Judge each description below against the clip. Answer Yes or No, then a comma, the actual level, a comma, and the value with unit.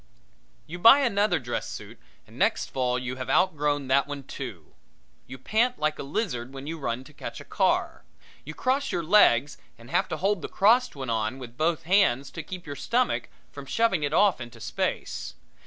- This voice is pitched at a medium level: Yes, medium, 150 Hz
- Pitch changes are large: Yes, wide, 7.3 semitones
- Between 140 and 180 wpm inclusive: No, average, 200 wpm